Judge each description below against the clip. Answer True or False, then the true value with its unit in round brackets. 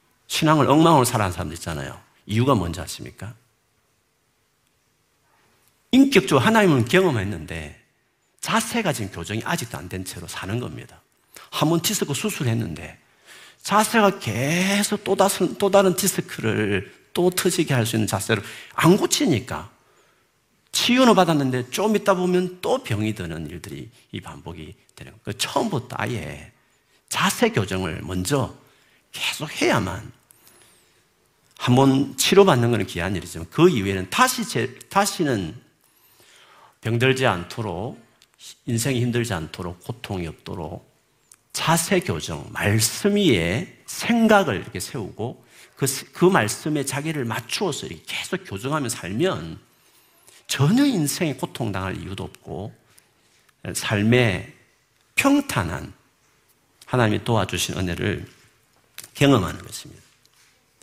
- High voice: False (125 Hz)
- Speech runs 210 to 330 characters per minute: True (265 characters per minute)